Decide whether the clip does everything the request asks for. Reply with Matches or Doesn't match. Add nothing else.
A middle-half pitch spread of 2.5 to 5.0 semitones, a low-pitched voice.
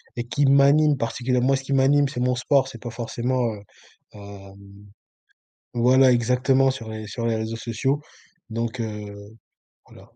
Matches